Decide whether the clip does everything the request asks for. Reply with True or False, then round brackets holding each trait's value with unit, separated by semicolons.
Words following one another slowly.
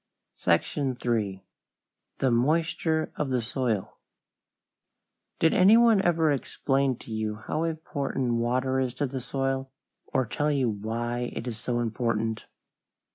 True (130 wpm)